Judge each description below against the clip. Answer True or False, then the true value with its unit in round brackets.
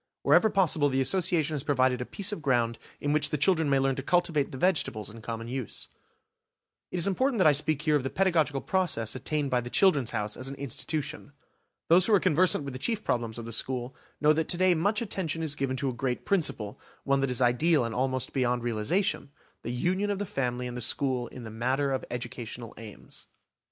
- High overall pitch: False (140 Hz)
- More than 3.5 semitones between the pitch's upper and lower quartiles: True (5.2 semitones)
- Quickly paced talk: True (220 wpm)